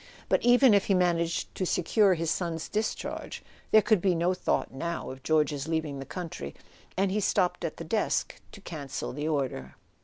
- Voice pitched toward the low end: No, medium, 170 Hz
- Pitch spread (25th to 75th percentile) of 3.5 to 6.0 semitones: Yes, average, 4.3 semitones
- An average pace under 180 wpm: No, average, 185 wpm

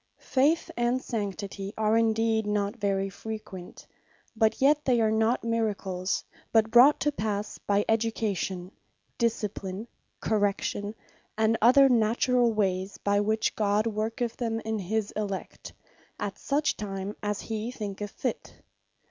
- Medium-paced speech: No, slow, 130 wpm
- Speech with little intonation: Yes, narrow, 2.1 semitones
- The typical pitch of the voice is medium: No, high, 215 Hz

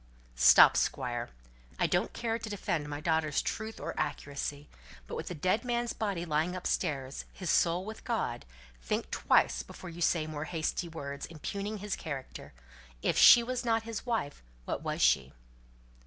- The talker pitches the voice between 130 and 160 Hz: No, medium, 170 Hz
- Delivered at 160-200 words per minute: Yes, average, 165 wpm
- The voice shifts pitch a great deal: Yes, wide, 6.8 semitones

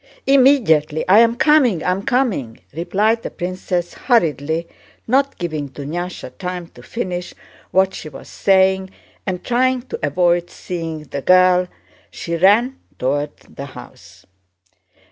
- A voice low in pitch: No, medium, 180 Hz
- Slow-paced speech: Yes, slow, 125 wpm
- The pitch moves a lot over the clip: Yes, wide, 6.0 semitones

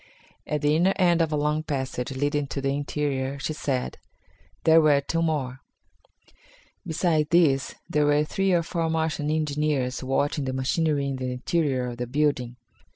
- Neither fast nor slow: Yes, average, 165 wpm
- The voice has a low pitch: No, medium, 145 Hz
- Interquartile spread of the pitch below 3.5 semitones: Yes, average, 2.8 semitones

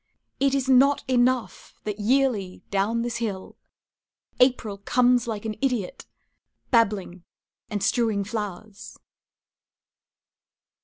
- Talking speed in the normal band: No, slow, 100 wpm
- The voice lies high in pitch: Yes, high, 225 Hz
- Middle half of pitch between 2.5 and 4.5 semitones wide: Yes, average, 3.7 semitones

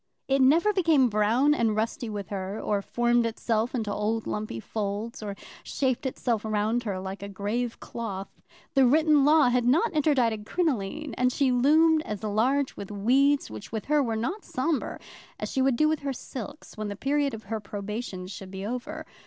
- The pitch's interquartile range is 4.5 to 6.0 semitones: Yes, average, 4.9 semitones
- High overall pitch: Yes, high, 240 Hz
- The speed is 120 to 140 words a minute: No, average, 185 wpm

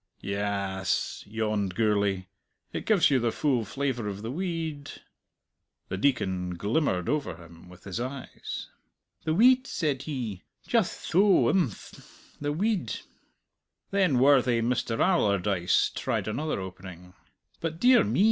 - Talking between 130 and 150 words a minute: Yes, slow, 135 wpm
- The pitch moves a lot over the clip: Yes, wide, 8.2 semitones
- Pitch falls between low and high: No, low, 120 Hz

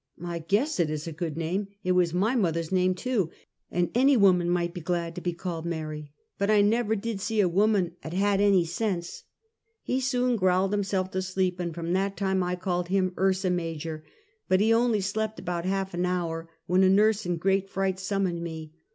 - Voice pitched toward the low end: No, medium, 185 Hz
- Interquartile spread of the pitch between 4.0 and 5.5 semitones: No, average, 2.7 semitones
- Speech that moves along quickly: Yes, fast, 215 wpm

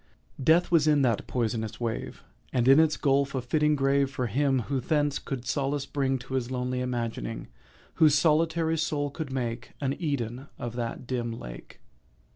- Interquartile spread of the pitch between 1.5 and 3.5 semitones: Yes, average, 3.2 semitones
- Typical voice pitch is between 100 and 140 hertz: Yes, low, 135 Hz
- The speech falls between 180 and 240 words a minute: No, average, 170 wpm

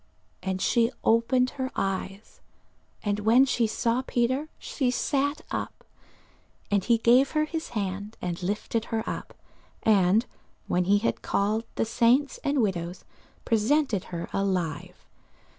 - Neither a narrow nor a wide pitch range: Yes, average, 4.6 semitones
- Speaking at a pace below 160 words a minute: Yes, slow, 135 wpm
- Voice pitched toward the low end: No, high, 225 Hz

